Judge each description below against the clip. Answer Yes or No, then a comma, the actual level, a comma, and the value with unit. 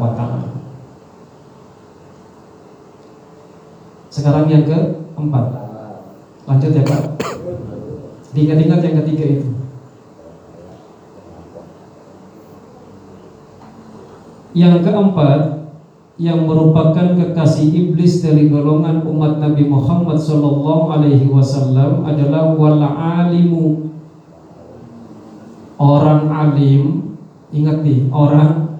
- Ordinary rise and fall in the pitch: No, narrow, 1.9 semitones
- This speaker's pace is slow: Yes, slow, 65 wpm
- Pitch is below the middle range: No, medium, 150 Hz